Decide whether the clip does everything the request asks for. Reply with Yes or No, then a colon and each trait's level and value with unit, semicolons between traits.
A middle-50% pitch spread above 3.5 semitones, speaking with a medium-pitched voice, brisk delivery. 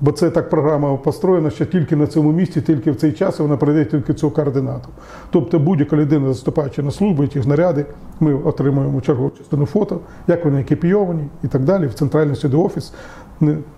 No: narrow, 2.4 semitones; medium, 155 Hz; fast, 185 wpm